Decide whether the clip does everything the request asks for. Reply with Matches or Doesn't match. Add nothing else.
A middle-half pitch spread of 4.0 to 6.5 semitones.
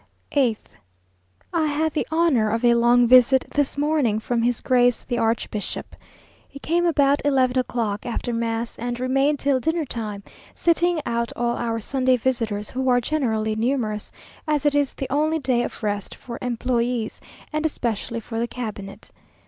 Doesn't match